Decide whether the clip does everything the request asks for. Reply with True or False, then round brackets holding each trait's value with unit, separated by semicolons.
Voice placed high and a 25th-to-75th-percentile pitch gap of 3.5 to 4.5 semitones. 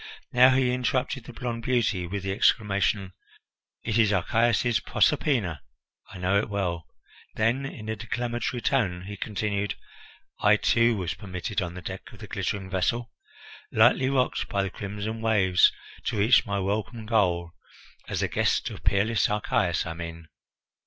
False (105 Hz; 3.8 semitones)